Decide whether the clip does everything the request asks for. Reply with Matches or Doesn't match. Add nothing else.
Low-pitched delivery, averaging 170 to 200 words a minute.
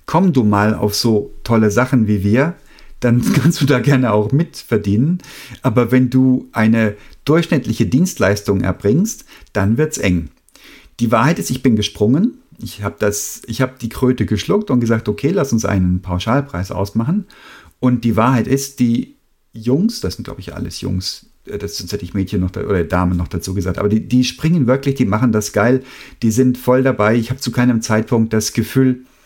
Matches